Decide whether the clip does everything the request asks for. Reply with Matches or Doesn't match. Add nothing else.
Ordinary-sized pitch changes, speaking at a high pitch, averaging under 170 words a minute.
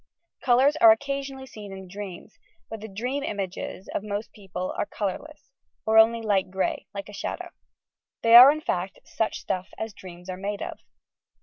Doesn't match